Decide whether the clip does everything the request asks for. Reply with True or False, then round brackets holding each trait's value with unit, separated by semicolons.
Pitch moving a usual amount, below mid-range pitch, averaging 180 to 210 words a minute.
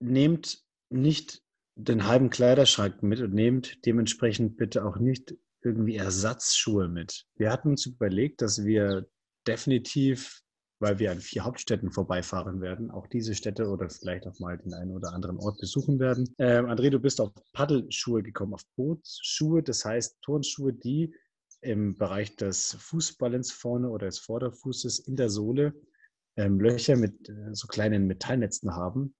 False (4.2 semitones; 115 Hz; 155 wpm)